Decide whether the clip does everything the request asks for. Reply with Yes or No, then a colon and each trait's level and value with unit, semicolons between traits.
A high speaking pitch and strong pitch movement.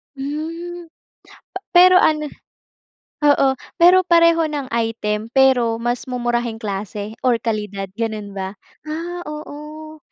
Yes: very high, 265 Hz; wide, 5.9 semitones